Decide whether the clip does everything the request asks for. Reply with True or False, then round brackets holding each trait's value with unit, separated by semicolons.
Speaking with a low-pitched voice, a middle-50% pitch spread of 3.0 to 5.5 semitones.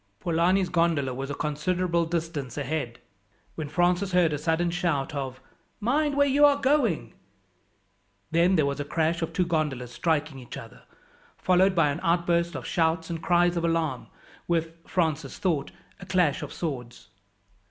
False (165 Hz; 3.3 semitones)